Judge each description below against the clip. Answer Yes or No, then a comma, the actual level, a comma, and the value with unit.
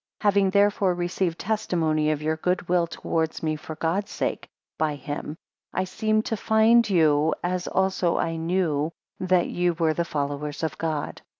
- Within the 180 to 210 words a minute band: No, average, 170 wpm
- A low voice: No, medium, 170 Hz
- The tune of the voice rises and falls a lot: No, average, 3.3 semitones